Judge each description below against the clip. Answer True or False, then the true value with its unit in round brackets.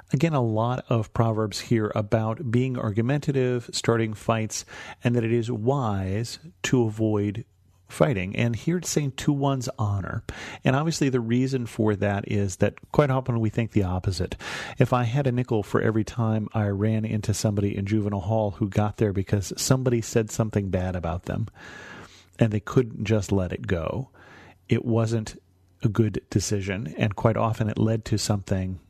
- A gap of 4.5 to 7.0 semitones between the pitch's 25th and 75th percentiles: False (2.9 semitones)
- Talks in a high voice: False (110 Hz)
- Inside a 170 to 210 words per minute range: True (175 wpm)